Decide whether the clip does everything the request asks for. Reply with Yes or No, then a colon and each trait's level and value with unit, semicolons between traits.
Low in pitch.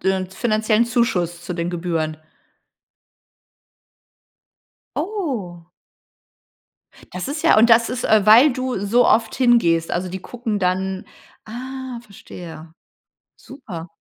No: high, 215 Hz